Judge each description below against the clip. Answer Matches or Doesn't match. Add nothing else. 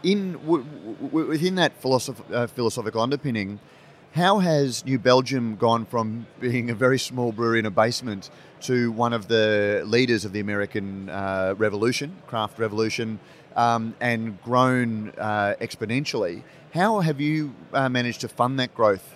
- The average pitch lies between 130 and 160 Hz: Doesn't match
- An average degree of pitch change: Matches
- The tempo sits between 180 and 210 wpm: Doesn't match